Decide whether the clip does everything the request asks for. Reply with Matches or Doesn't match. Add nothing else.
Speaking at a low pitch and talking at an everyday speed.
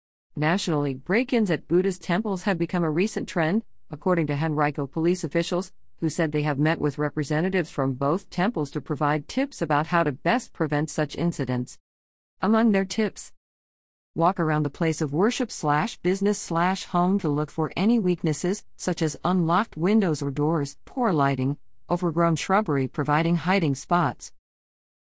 Doesn't match